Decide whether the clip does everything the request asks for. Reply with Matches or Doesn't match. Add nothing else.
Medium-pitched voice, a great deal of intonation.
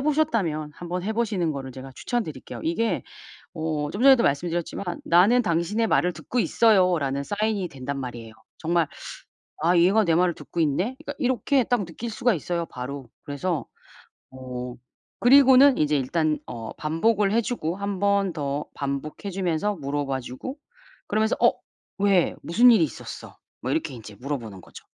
Matches